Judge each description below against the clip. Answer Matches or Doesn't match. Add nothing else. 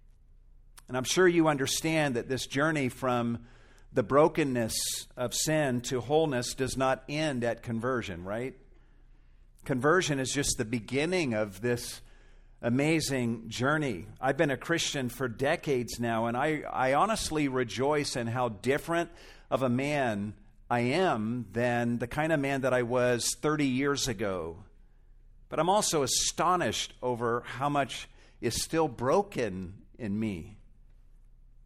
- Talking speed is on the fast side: Doesn't match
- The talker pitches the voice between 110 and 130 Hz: Matches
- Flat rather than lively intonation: Doesn't match